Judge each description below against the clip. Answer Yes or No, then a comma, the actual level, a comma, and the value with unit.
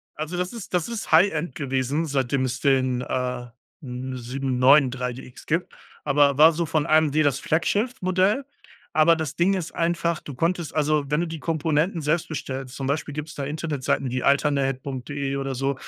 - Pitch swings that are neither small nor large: Yes, average, 3.7 semitones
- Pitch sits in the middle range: Yes, medium, 145 Hz